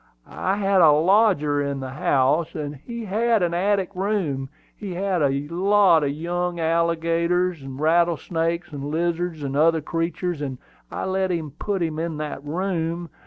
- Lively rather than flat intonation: No, average, 3.5 semitones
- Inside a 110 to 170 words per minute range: Yes, average, 155 wpm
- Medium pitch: Yes, medium, 170 Hz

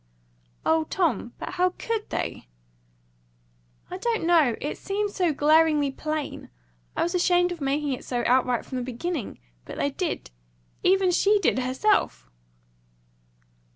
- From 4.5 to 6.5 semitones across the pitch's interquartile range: Yes, average, 5.2 semitones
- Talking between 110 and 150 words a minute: Yes, average, 140 wpm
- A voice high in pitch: Yes, very high, 320 Hz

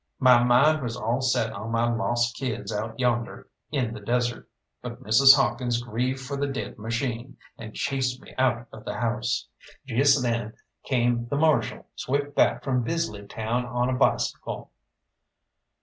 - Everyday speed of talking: Yes, average, 160 wpm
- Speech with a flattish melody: Yes, narrow, 2.3 semitones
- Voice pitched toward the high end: No, low, 120 Hz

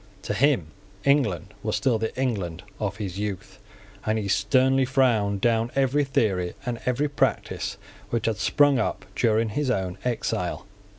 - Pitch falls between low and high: No, low, 115 Hz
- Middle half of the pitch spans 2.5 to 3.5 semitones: No, average, 4.5 semitones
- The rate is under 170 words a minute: Yes, average, 155 wpm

